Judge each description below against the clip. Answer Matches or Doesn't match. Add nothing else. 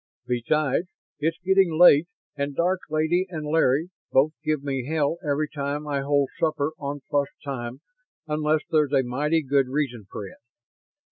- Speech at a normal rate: Matches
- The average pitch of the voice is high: Doesn't match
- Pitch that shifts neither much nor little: Doesn't match